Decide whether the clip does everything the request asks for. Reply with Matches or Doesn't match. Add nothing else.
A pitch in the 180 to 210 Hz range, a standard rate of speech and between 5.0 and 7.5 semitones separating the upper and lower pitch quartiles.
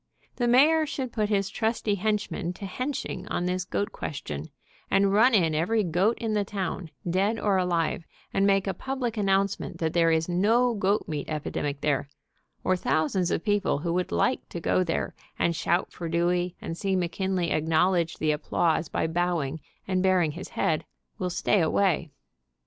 Doesn't match